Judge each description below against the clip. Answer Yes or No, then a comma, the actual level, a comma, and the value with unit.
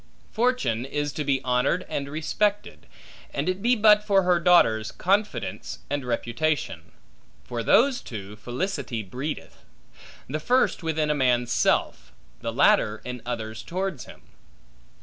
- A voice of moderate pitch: Yes, medium, 150 Hz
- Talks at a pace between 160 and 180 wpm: No, slow, 135 wpm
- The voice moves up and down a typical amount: No, wide, 7.6 semitones